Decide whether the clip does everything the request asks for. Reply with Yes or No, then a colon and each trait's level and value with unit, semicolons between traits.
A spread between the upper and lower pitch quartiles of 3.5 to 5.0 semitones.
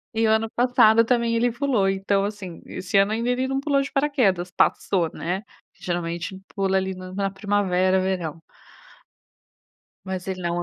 Yes: average, 3.9 semitones